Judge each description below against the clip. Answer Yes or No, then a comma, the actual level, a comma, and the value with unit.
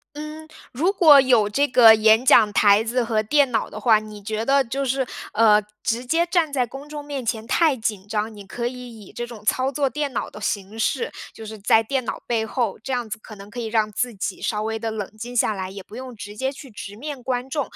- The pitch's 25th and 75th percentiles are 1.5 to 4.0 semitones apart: Yes, average, 3.7 semitones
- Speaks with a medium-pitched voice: No, high, 235 Hz